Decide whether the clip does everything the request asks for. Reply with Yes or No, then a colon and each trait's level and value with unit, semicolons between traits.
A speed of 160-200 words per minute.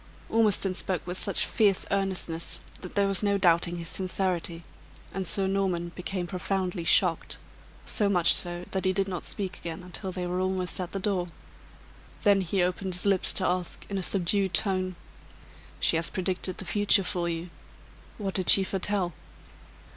Yes: average, 170 wpm